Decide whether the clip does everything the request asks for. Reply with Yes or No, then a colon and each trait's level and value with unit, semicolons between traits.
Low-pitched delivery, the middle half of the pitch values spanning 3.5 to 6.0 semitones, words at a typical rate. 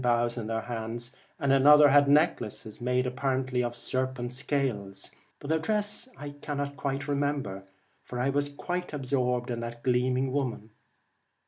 No: low, 130 Hz; average, 2.9 semitones; average, 160 wpm